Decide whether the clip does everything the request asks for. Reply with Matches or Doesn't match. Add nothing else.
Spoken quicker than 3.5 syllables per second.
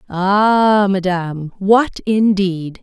Doesn't match